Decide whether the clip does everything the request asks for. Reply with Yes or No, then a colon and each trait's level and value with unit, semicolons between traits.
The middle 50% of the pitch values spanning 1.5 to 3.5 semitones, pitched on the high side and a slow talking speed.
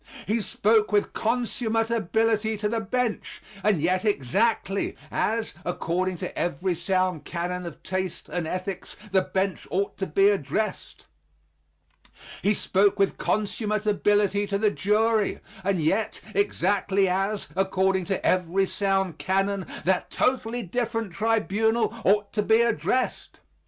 Yes: average, 2.7 semitones; high, 200 Hz; slow, 130 wpm